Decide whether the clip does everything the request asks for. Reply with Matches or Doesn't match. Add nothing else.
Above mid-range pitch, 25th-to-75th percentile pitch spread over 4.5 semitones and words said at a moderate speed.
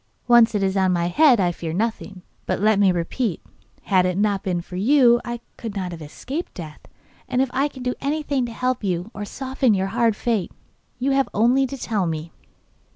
Doesn't match